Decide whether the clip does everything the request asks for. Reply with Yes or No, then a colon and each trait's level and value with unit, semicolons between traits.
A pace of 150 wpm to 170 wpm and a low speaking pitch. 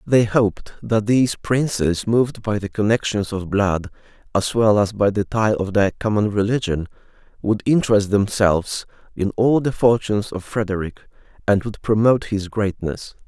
Yes: average, 160 wpm; low, 105 Hz